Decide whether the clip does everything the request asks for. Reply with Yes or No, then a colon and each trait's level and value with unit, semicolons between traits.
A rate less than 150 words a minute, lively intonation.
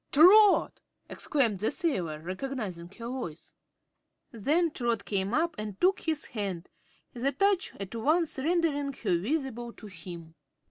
Yes: slow, 135 wpm; wide, 8.0 semitones